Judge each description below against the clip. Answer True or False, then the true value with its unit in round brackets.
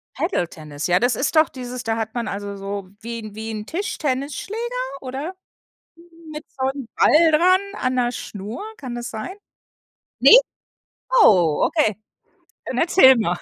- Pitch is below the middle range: False (245 Hz)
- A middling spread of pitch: False (6.1 semitones)